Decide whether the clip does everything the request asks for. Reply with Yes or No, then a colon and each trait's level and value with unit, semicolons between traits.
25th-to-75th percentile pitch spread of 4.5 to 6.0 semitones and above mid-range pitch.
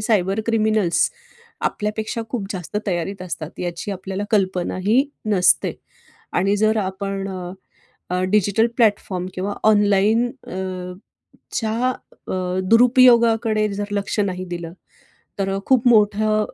No: average, 2.7 semitones; high, 205 Hz